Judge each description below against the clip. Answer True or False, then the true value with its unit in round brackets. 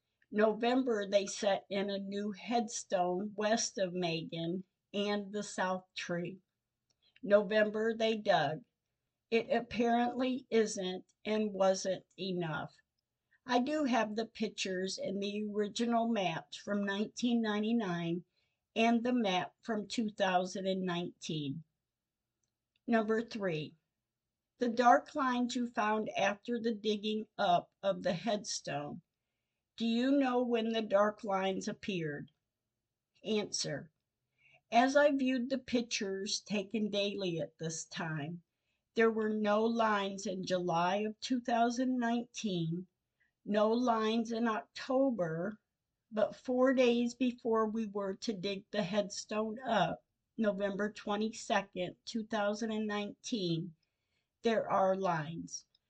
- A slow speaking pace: True (115 wpm)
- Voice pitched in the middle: False (205 Hz)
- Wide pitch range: False (3.9 semitones)